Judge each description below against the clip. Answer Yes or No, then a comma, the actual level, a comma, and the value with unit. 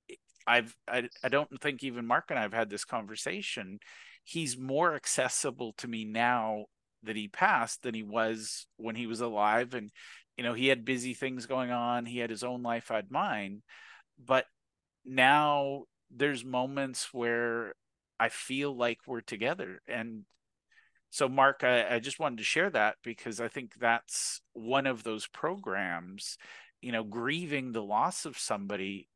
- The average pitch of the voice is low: Yes, low, 120 Hz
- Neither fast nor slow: Yes, average, 165 wpm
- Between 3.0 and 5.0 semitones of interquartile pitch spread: No, narrow, 2.6 semitones